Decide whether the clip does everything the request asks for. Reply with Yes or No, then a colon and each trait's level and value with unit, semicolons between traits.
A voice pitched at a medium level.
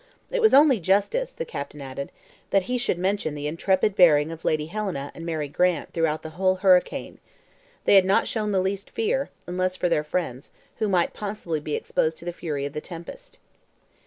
Yes: medium, 180 Hz